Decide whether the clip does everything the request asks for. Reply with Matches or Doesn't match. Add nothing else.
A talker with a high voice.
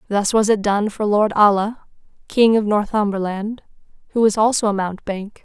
Matches